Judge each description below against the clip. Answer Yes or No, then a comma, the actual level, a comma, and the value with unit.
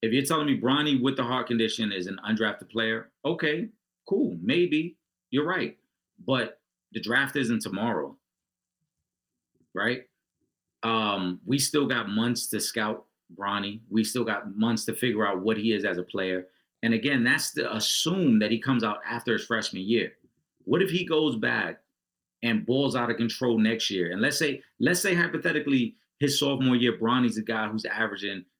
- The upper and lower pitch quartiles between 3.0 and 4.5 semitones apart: Yes, average, 3.8 semitones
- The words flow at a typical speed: Yes, average, 175 wpm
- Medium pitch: No, low, 115 Hz